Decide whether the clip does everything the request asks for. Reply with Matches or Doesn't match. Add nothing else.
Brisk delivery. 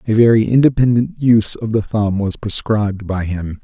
Doesn't match